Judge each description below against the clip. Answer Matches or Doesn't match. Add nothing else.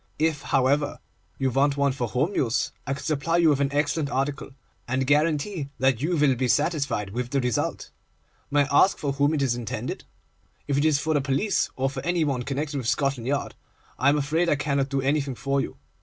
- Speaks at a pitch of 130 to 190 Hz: Matches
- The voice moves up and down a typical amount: Doesn't match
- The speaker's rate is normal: Doesn't match